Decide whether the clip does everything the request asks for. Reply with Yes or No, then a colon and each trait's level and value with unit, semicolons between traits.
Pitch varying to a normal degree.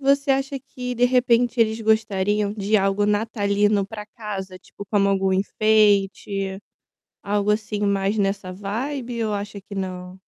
No: narrow, 2.2 semitones